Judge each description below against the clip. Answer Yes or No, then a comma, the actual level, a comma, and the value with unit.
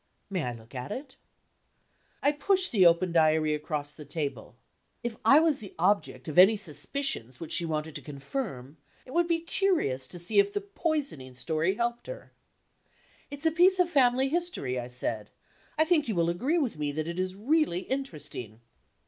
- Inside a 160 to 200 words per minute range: Yes, average, 180 wpm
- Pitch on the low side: No, medium, 185 Hz